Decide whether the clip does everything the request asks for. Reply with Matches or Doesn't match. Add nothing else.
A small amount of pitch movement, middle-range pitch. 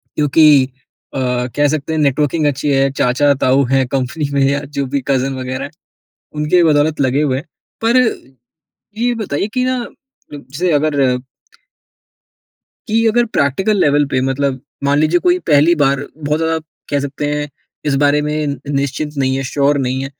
Matches